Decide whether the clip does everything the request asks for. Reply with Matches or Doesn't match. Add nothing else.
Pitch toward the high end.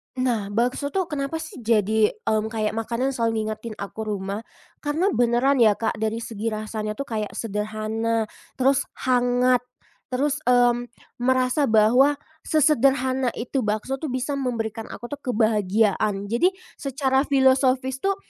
Matches